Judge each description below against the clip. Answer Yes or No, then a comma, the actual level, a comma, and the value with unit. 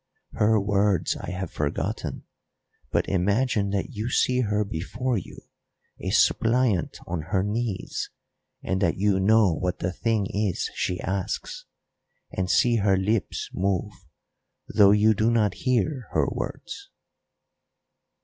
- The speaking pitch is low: Yes, low, 105 Hz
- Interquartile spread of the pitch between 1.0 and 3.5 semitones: Yes, average, 3.0 semitones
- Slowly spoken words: Yes, slow, 130 wpm